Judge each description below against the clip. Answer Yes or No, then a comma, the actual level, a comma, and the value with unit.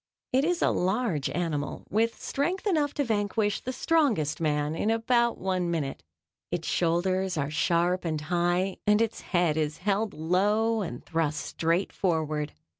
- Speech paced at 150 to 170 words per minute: Yes, average, 155 wpm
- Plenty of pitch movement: Yes, wide, 5.7 semitones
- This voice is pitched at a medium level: Yes, medium, 180 Hz